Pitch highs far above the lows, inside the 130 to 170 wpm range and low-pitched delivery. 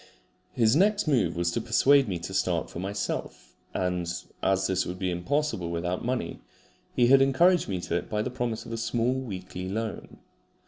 No: wide, 5.9 semitones; average, 185 wpm; low, 105 Hz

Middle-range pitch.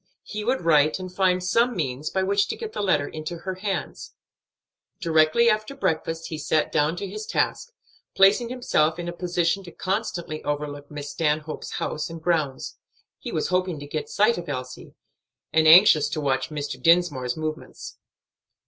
Yes: medium, 165 Hz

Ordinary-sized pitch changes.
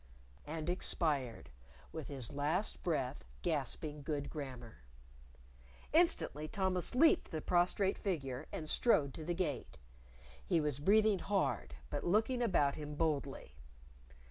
Yes: average, 4.8 semitones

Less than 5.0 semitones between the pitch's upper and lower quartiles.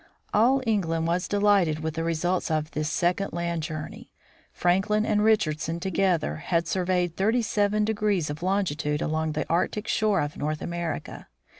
Yes: average, 4.3 semitones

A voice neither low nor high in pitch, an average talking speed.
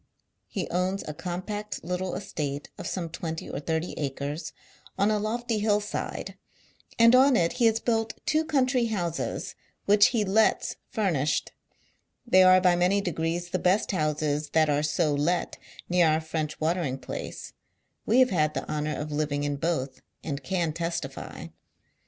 Yes: medium, 175 Hz; average, 160 wpm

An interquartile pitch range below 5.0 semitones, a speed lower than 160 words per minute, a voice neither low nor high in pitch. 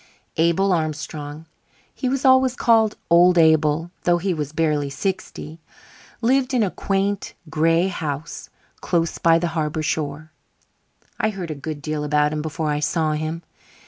Yes: average, 3.6 semitones; average, 150 wpm; medium, 165 Hz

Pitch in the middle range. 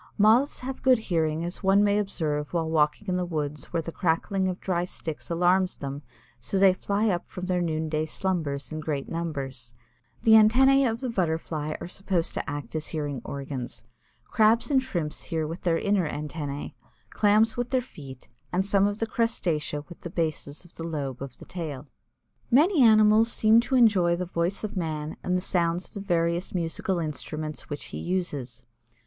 Yes: medium, 175 Hz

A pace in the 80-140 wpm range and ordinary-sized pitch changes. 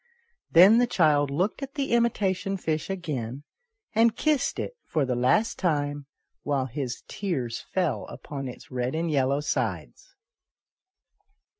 No: slow, 135 wpm; wide, 6.5 semitones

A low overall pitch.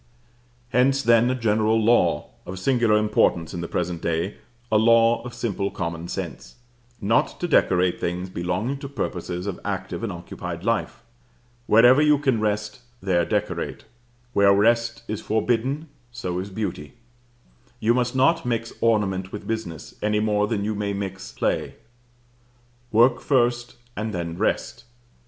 Yes: low, 105 Hz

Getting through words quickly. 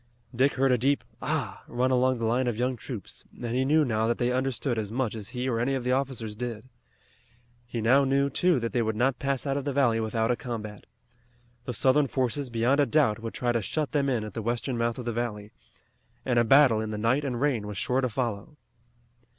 Yes: fast, 235 wpm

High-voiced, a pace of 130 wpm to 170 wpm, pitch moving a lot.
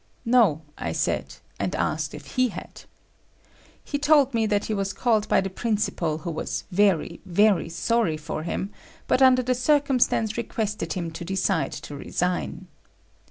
Yes: high, 205 Hz; average, 160 wpm; wide, 5.7 semitones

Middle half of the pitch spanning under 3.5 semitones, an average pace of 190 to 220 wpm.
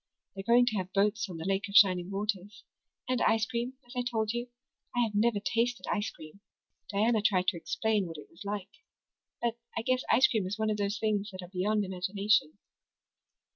Yes: average, 2.8 semitones; fast, 205 wpm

